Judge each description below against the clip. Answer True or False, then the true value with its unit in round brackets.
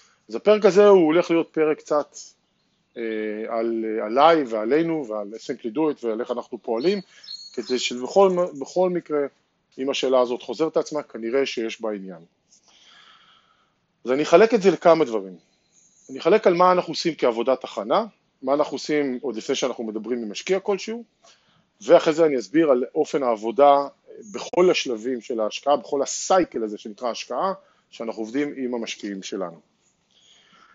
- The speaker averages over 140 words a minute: True (150 wpm)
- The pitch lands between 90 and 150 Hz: True (140 Hz)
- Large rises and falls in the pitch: True (6.7 semitones)